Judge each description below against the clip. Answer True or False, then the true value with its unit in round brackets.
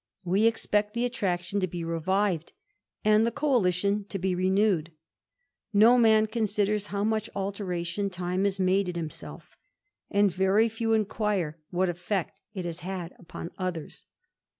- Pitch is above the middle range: True (195 Hz)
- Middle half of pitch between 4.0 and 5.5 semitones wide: False (2.9 semitones)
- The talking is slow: True (130 wpm)